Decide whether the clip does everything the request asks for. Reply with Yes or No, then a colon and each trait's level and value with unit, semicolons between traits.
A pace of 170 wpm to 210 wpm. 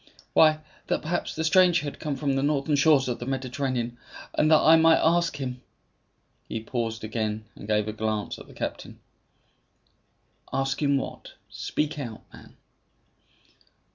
No: average, 160 wpm